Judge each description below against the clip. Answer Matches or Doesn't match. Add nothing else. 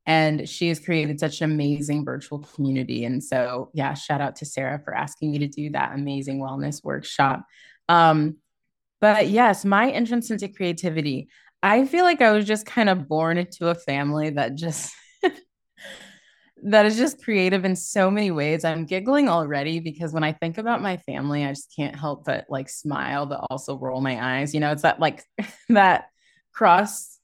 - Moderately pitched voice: Matches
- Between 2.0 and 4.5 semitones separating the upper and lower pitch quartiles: Doesn't match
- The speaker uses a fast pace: Doesn't match